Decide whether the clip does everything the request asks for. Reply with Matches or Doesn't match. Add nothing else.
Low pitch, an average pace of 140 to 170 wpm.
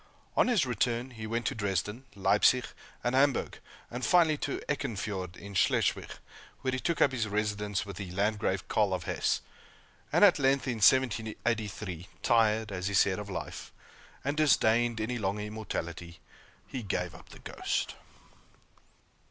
Matches